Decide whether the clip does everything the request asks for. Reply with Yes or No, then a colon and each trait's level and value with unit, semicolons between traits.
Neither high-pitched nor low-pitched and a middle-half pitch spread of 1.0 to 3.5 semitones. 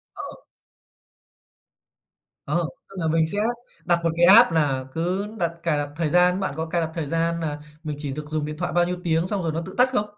Yes: medium, 165 Hz; narrow, 2.5 semitones